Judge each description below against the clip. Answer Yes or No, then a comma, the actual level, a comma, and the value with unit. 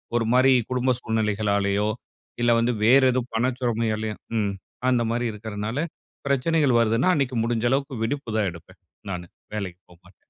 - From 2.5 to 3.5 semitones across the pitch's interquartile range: Yes, average, 3.1 semitones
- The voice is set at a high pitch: No, low, 115 Hz